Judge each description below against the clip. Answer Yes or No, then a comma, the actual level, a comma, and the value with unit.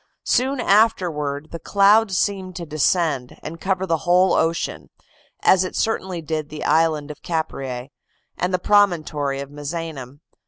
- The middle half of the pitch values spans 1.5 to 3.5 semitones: No, average, 4.1 semitones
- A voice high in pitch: No, medium, 165 Hz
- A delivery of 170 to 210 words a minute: No, average, 145 wpm